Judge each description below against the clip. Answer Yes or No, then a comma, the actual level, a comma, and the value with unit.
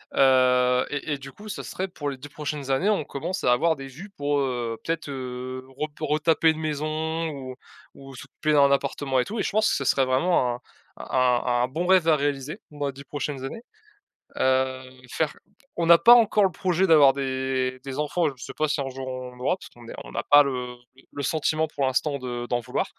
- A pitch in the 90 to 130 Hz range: No, medium, 140 Hz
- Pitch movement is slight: No, average, 3.3 semitones